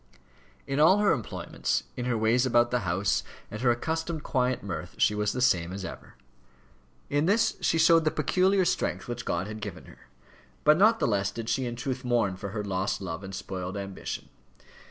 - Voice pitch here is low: Yes, low, 120 Hz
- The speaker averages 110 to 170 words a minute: No, average, 195 wpm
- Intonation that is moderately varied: No, wide, 7.3 semitones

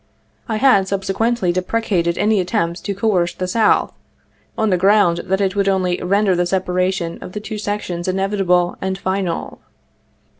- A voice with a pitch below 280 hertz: Yes, high, 190 Hz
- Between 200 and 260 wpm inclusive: No, average, 160 wpm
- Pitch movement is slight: Yes, narrow, 2.3 semitones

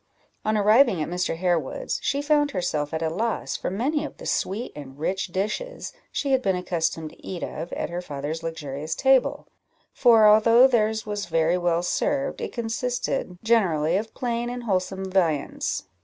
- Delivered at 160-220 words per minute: Yes, average, 170 wpm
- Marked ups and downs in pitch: Yes, wide, 6.2 semitones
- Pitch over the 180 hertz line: Yes, high, 190 Hz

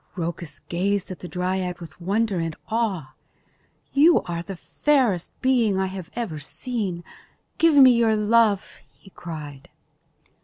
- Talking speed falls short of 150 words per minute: Yes, average, 140 wpm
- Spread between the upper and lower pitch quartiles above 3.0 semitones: Yes, average, 5.0 semitones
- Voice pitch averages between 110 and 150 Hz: No, high, 190 Hz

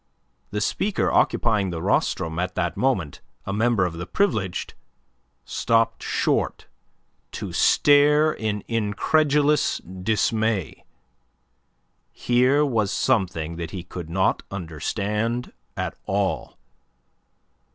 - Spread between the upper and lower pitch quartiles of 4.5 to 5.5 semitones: Yes, average, 5.0 semitones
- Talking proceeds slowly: Yes, slow, 100 wpm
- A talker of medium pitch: No, low, 105 Hz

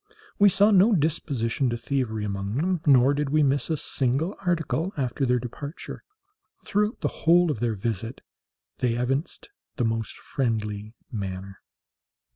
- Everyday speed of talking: Yes, average, 145 wpm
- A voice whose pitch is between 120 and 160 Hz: Yes, low, 135 Hz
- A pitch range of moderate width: No, wide, 6.1 semitones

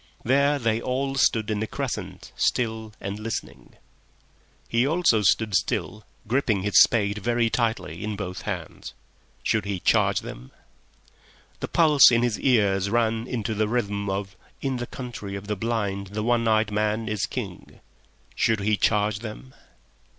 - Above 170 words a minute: No, average, 155 wpm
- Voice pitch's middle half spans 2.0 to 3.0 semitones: Yes, average, 2.7 semitones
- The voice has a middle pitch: No, low, 110 Hz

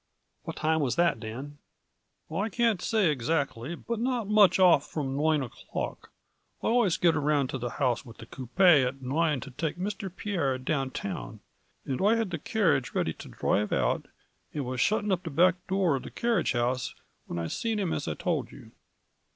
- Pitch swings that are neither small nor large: No, wide, 6.7 semitones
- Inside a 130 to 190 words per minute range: No, fast, 205 wpm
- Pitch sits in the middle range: Yes, medium, 155 Hz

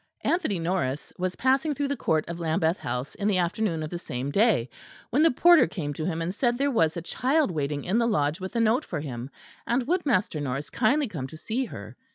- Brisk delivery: Yes, fast, 230 wpm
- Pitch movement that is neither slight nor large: No, wide, 8.0 semitones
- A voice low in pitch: No, medium, 185 Hz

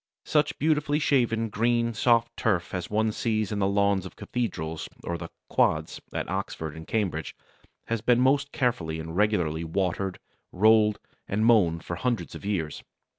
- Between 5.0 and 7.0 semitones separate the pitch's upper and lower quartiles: Yes, wide, 5.4 semitones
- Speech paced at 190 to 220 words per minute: No, average, 160 wpm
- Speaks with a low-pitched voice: Yes, low, 105 Hz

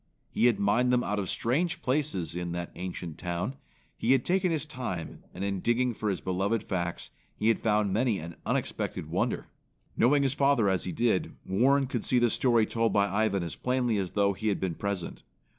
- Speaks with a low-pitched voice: Yes, low, 110 Hz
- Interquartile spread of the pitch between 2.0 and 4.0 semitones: No, average, 4.9 semitones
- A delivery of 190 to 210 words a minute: Yes, fast, 205 wpm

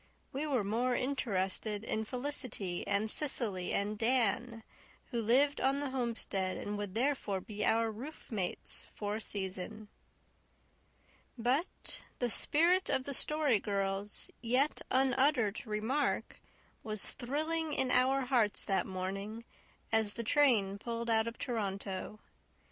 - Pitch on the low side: No, high, 230 Hz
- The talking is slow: Yes, slow, 125 wpm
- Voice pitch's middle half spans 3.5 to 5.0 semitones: Yes, average, 4.3 semitones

